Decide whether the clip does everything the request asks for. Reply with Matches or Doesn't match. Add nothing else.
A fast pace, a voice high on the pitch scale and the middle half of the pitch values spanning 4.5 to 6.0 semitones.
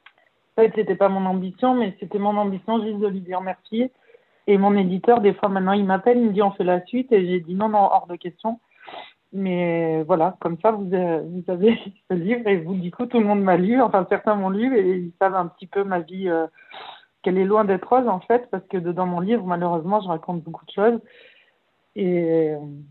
Doesn't match